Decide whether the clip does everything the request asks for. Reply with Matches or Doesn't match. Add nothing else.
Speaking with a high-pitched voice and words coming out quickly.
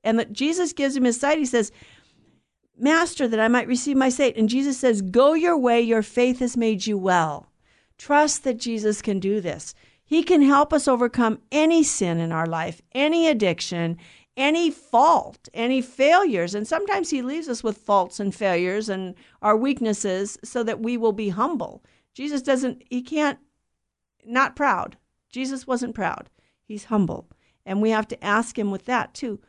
Doesn't match